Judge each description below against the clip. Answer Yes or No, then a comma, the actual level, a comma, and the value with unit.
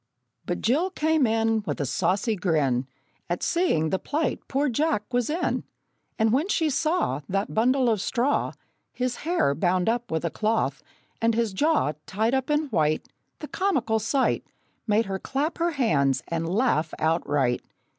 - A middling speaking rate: Yes, average, 165 wpm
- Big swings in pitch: Yes, wide, 8.3 semitones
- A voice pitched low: No, high, 225 Hz